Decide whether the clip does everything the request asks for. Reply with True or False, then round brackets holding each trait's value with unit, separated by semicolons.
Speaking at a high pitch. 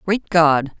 False (165 Hz)